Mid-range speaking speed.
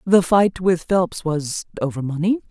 Yes: average, 170 wpm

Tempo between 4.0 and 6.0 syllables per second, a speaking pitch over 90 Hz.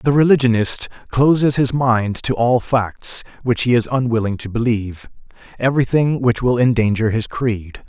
Yes: 4.8 syllables/s; low, 120 Hz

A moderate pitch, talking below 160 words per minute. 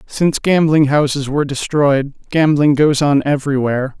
Yes: medium, 145 Hz; slow, 135 wpm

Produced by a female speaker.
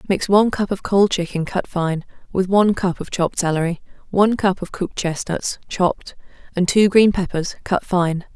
Yes: female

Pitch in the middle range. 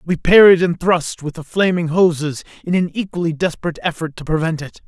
Yes: medium, 170 Hz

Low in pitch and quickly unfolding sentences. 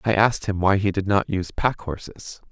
Yes: low, 100 Hz; fast, 240 wpm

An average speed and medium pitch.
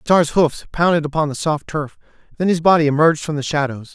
No: fast, 215 wpm; medium, 155 Hz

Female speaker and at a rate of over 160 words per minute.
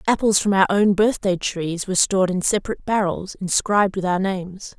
Yes: female; average, 200 wpm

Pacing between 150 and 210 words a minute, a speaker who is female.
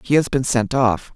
No: fast, 260 wpm; female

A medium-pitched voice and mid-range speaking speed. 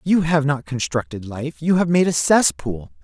Yes: medium, 145 Hz; average, 180 wpm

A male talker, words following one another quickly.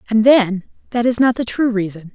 No: female; fast, 225 wpm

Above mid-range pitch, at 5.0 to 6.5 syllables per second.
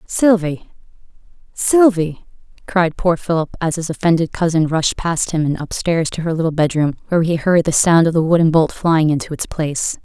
No: medium, 165 Hz; 5.2 syllables/s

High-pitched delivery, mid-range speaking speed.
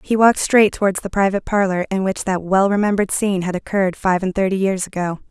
No: high, 195 Hz; fast, 225 wpm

